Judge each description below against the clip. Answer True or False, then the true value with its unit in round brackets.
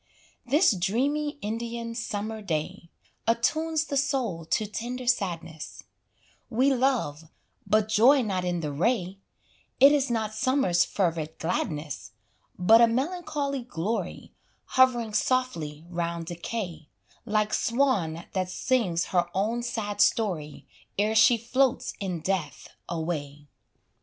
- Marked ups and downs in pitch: True (6.4 semitones)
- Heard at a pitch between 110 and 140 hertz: False (215 Hz)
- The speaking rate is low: True (115 wpm)